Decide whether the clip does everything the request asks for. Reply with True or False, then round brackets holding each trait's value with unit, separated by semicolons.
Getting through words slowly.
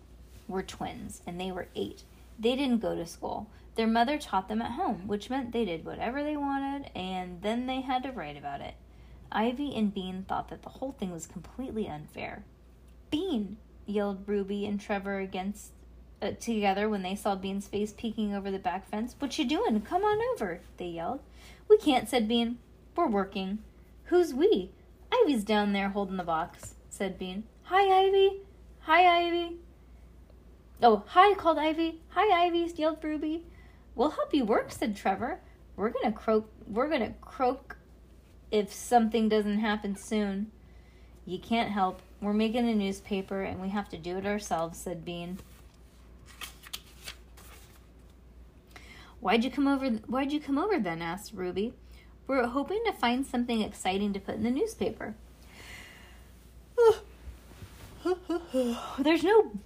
False (155 wpm)